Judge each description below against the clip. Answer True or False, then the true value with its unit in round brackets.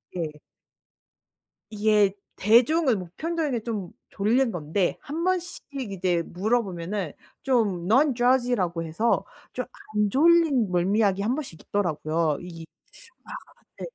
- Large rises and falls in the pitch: True (6.3 semitones)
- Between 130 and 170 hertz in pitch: False (210 Hz)